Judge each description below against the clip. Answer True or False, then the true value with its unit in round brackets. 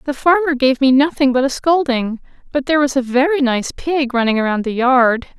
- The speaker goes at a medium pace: False (210 wpm)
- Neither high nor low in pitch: False (270 Hz)